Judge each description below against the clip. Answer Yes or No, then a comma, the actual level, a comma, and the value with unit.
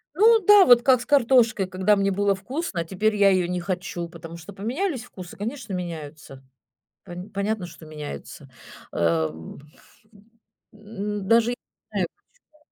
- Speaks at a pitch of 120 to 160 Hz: No, high, 195 Hz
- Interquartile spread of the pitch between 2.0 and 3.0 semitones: No, wide, 5.6 semitones